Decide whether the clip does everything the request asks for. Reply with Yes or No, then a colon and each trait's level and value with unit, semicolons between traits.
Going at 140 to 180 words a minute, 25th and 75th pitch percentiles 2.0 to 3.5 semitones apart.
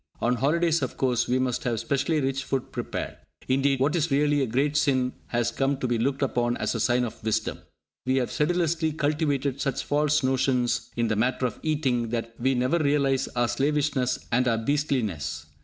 No: average, 190 wpm; average, 3.1 semitones